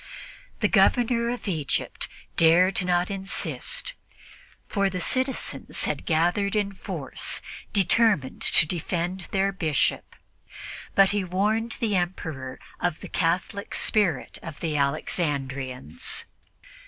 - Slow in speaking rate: Yes, slow, 110 wpm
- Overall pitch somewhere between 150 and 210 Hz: Yes, medium, 185 Hz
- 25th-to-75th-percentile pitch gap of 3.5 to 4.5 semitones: Yes, average, 4.0 semitones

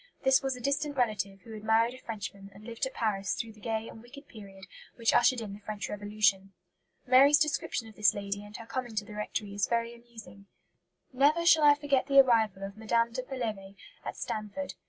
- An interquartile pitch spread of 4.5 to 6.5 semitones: No, average, 3.9 semitones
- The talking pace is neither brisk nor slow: No, fast, 210 wpm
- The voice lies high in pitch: Yes, high, 225 Hz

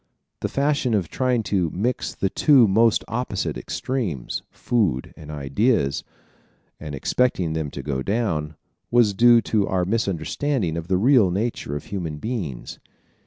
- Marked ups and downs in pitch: Yes, wide, 7.2 semitones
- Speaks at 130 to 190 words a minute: Yes, average, 145 wpm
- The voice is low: Yes, low, 100 Hz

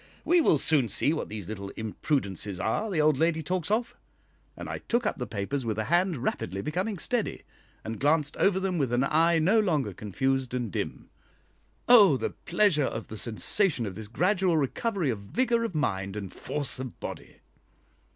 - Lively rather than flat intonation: Yes, wide, 8.8 semitones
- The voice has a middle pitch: Yes, medium, 145 Hz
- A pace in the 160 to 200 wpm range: Yes, average, 185 wpm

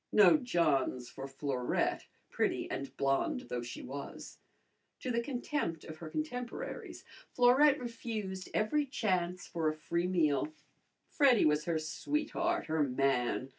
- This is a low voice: No, medium, 180 Hz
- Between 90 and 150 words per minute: Yes, slow, 135 wpm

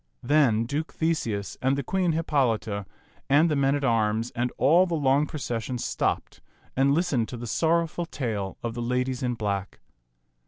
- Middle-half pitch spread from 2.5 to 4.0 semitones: No, average, 4.9 semitones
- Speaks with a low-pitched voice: Yes, low, 130 Hz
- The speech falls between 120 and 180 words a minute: Yes, average, 165 wpm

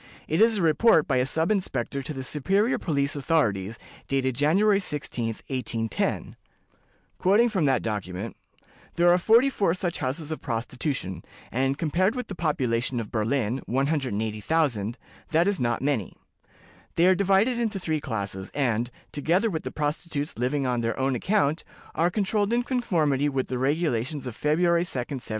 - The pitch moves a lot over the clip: Yes, wide, 6.1 semitones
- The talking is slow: No, average, 150 wpm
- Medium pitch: Yes, medium, 145 Hz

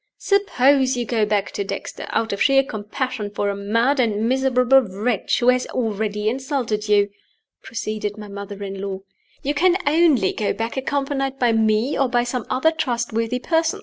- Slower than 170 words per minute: No, average, 175 wpm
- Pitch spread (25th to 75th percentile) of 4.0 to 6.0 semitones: Yes, average, 4.3 semitones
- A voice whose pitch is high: Yes, high, 240 Hz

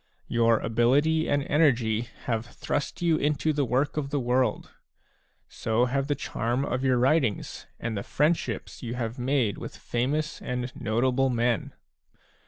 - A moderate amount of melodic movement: Yes, average, 3.4 semitones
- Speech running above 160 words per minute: No, average, 150 wpm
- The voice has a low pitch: Yes, low, 125 Hz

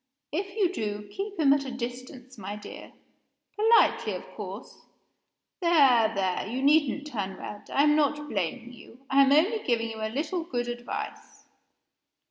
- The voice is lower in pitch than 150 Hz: No, very high, 265 Hz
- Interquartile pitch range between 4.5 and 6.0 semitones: Yes, average, 5.0 semitones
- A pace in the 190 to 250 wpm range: No, average, 160 wpm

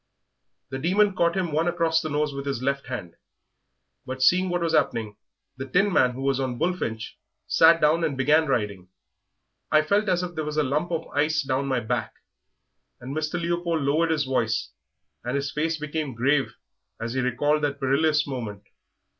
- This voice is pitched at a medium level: Yes, medium, 145 Hz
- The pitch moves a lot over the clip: No, average, 4.0 semitones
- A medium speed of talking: Yes, average, 180 wpm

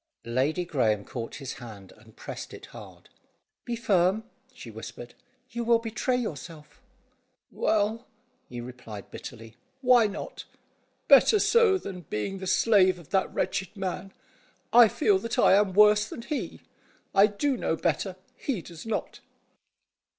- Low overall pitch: No, high, 190 Hz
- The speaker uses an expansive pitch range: Yes, wide, 8.8 semitones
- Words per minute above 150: No, average, 145 wpm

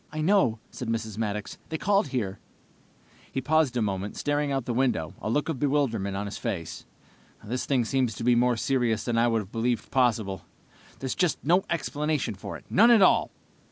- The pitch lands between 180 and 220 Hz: No, low, 125 Hz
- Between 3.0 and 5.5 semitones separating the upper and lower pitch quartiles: Yes, average, 4.9 semitones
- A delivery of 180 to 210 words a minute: Yes, average, 195 wpm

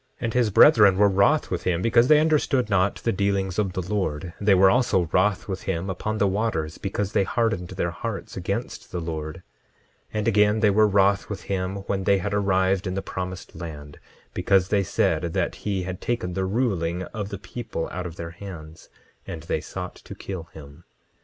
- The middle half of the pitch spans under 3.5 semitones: Yes, narrow, 2.6 semitones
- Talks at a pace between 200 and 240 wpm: Yes, fast, 205 wpm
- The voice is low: Yes, very low, 95 Hz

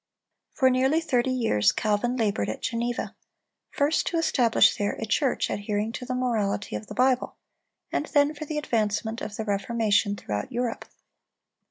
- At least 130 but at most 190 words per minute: Yes, average, 160 wpm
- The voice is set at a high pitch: Yes, high, 235 Hz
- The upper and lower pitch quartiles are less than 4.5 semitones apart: Yes, average, 3.8 semitones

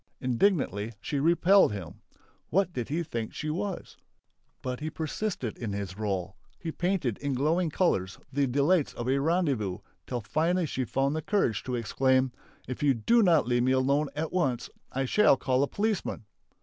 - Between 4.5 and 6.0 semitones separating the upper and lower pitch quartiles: Yes, wide, 5.6 semitones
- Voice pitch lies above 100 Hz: Yes, medium, 140 Hz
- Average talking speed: Yes, average, 170 wpm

